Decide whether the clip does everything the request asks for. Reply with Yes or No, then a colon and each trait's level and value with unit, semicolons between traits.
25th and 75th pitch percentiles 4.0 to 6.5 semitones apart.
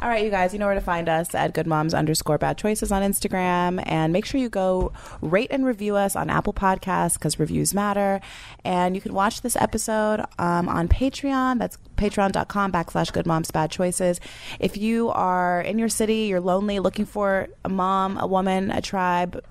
No: average, 2.8 semitones